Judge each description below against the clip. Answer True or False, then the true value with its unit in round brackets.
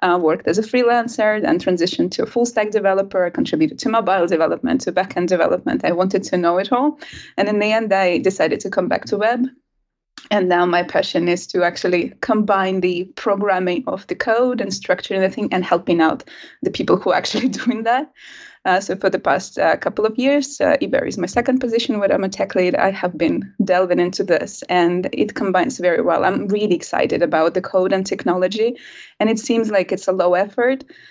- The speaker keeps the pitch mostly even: False (4.8 semitones)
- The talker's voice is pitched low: False (195 Hz)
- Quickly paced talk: True (215 wpm)